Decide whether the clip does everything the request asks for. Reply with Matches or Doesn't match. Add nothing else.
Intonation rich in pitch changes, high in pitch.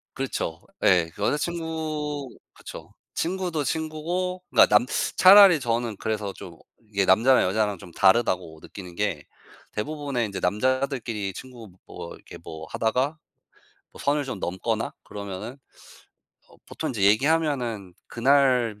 Doesn't match